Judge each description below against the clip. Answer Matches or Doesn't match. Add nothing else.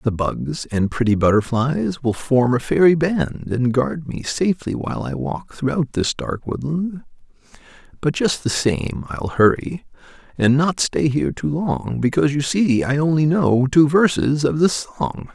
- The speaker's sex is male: Matches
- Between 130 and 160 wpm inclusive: Doesn't match